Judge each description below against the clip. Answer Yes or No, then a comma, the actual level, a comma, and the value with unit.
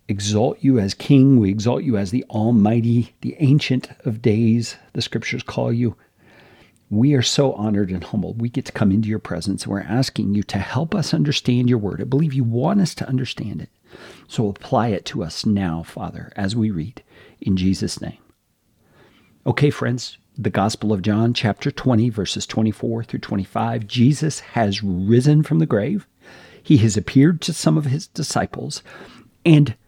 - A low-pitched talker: Yes, low, 115 Hz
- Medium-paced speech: Yes, average, 175 wpm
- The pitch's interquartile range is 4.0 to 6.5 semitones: Yes, average, 4.3 semitones